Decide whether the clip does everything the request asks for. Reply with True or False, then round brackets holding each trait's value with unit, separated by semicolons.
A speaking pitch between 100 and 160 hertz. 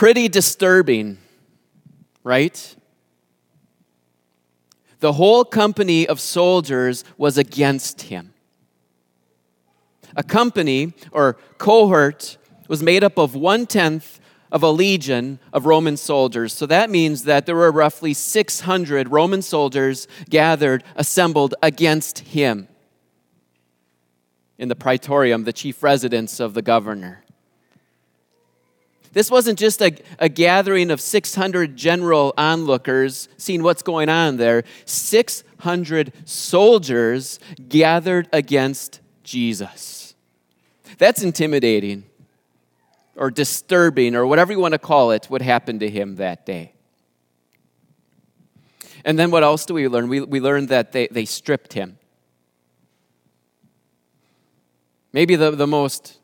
True (140 Hz)